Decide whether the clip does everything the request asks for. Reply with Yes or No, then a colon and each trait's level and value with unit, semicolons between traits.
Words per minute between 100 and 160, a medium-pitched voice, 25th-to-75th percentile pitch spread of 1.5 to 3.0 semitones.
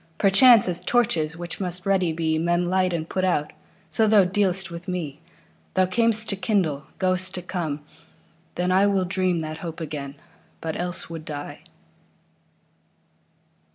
Yes: average, 140 wpm; medium, 180 Hz; average, 2.7 semitones